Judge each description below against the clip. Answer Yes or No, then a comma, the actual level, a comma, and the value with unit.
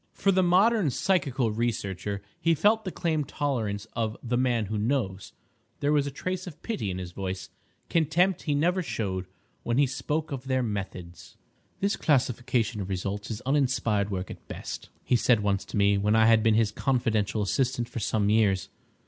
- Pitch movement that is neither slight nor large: No, wide, 5.9 semitones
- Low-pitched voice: Yes, low, 120 Hz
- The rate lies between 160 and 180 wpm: Yes, average, 175 wpm